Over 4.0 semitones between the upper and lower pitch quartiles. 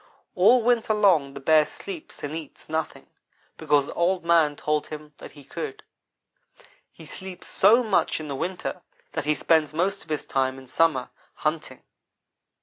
Yes: average, 4.4 semitones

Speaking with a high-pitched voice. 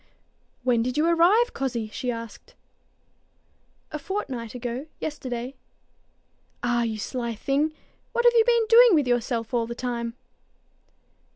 Yes: very high, 250 Hz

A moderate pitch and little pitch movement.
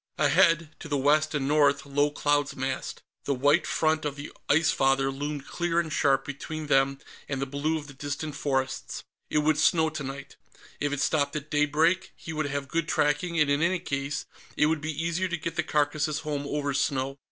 Yes: medium, 145 Hz; narrow, 1.9 semitones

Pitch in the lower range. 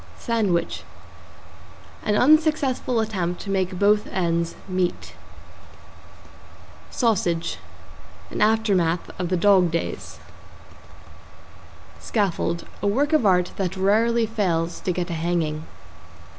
No: high, 190 Hz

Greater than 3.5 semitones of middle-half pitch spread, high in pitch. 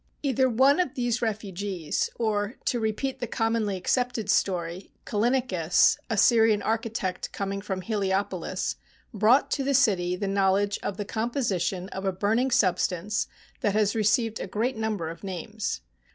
No: average, 3.2 semitones; high, 210 Hz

